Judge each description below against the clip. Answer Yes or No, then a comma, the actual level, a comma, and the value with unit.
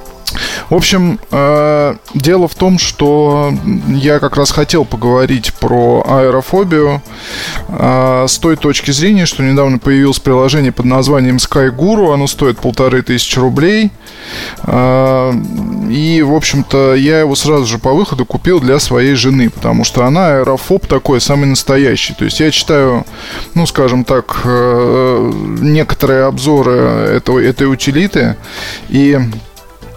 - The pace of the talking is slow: No, average, 130 wpm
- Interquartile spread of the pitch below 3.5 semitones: Yes, average, 2.7 semitones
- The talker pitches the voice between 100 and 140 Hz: Yes, low, 135 Hz